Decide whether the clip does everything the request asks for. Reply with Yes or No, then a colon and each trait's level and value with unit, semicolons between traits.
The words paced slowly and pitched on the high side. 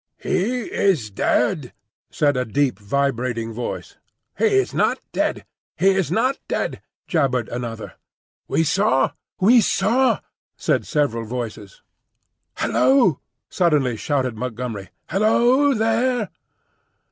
No: slow, 110 wpm; medium, 150 Hz